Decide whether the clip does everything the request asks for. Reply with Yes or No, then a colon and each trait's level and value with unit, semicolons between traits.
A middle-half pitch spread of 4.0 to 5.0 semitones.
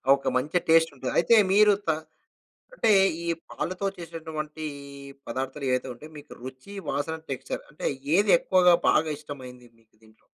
Yes: average, 4.4 semitones